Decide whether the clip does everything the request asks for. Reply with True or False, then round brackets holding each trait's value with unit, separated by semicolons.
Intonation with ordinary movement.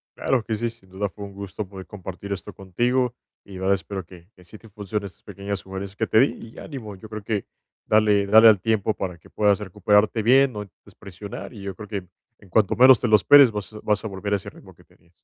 False (2.3 semitones)